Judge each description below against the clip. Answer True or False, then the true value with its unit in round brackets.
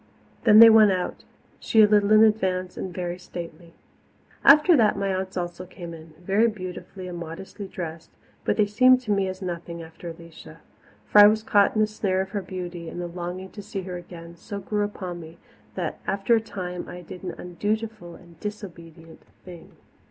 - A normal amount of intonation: True (3.2 semitones)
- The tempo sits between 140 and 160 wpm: False (195 wpm)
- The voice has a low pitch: False (185 Hz)